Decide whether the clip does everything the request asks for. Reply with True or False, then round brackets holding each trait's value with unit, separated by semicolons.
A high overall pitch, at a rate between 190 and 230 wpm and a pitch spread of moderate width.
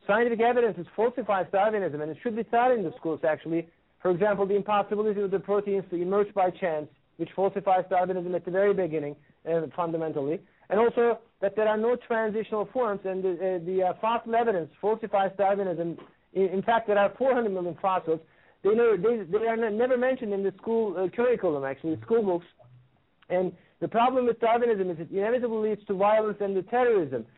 True (200 Hz; 195 wpm; 4.3 semitones)